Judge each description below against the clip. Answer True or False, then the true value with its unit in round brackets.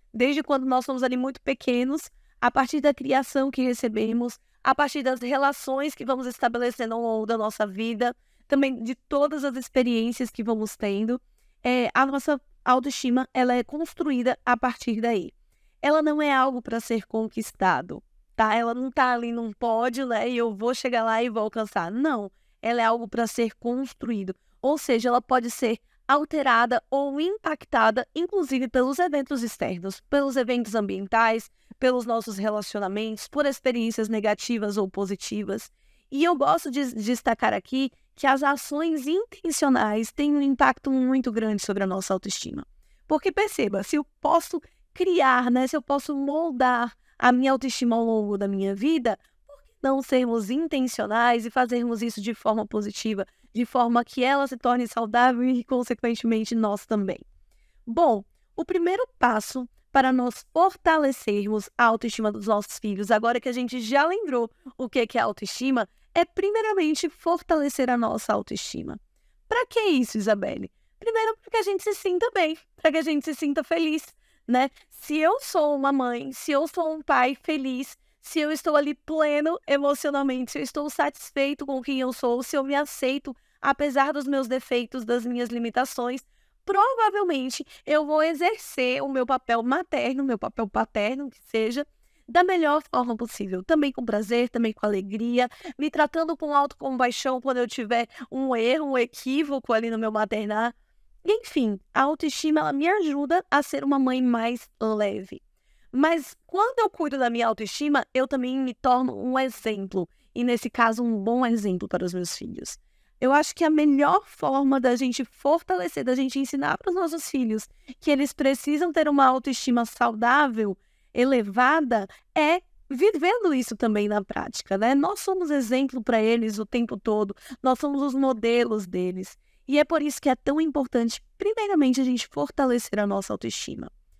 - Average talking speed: True (165 wpm)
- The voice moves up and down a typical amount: True (3.9 semitones)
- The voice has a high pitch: True (255 Hz)